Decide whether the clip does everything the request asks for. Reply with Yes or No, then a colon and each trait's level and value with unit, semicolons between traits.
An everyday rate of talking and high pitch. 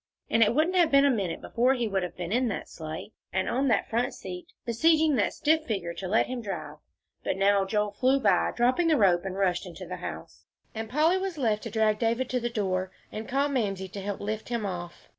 No: fast, 235 wpm; high, 220 Hz